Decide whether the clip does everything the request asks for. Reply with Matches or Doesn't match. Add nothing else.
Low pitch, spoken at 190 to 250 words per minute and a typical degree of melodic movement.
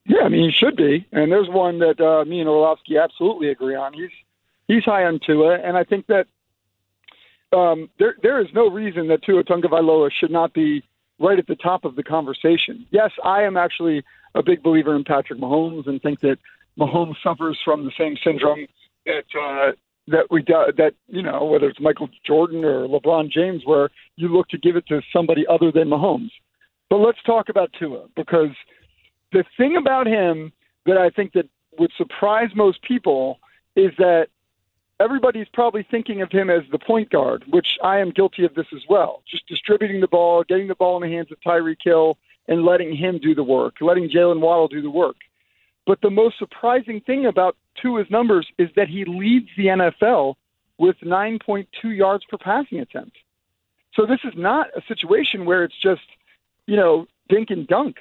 Doesn't match